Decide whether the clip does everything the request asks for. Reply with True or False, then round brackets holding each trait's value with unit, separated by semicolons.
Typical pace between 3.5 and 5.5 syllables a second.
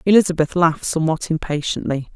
False (6.5 syllables/s)